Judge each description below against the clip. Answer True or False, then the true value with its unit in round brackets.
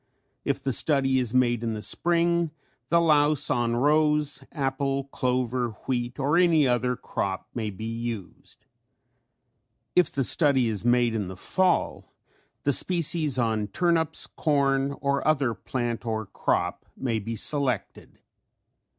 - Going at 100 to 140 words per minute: True (135 wpm)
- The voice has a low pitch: True (130 Hz)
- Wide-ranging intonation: False (4.1 semitones)